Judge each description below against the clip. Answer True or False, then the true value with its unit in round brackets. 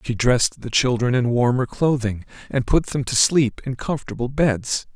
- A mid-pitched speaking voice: False (125 Hz)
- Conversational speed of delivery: True (180 wpm)